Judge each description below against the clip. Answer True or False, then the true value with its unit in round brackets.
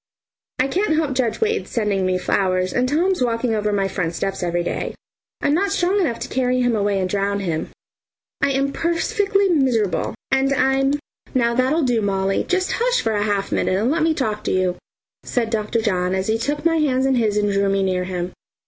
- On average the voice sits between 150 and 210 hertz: False (230 Hz)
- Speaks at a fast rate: True (210 wpm)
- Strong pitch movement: True (6.3 semitones)